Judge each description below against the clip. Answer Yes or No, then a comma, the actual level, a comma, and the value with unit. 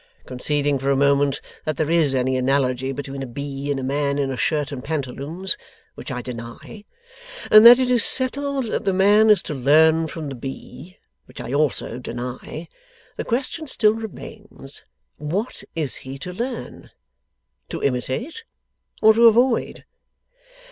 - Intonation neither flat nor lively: No, wide, 7.8 semitones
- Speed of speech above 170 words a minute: No, average, 160 wpm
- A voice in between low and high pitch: Yes, medium, 145 Hz